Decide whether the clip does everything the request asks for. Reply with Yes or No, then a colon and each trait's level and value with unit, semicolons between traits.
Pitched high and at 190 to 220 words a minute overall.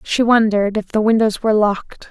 Yes: high, 215 Hz; average, 200 wpm